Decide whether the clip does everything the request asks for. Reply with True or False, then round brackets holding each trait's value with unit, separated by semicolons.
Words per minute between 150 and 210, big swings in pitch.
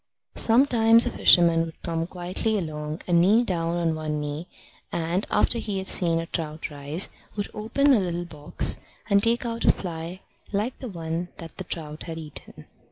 False (180 wpm; 4.4 semitones)